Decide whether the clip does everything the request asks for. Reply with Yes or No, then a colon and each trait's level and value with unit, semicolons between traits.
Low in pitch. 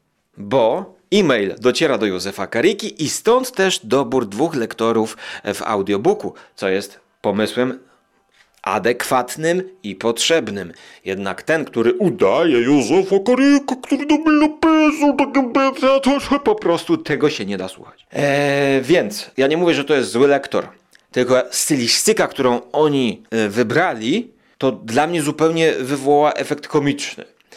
No: medium, 145 Hz